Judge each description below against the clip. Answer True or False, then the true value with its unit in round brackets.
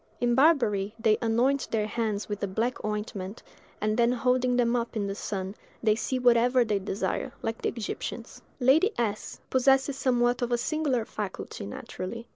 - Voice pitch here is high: True (235 Hz)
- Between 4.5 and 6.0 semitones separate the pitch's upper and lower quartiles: False (2.9 semitones)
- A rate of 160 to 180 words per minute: True (170 wpm)